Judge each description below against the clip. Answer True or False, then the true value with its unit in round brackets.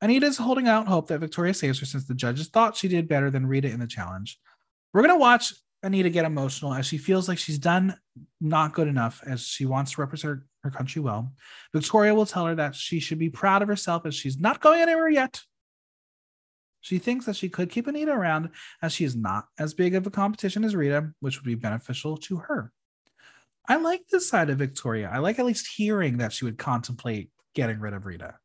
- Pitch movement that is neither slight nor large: False (6.9 semitones)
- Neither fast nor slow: False (225 wpm)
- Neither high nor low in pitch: True (160 Hz)